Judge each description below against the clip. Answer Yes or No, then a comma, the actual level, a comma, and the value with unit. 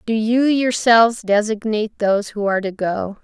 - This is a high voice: Yes, high, 215 Hz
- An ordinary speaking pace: Yes, average, 165 wpm